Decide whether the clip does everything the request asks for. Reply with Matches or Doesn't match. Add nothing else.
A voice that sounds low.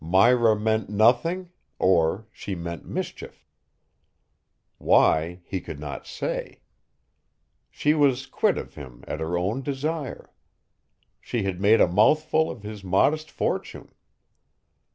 Matches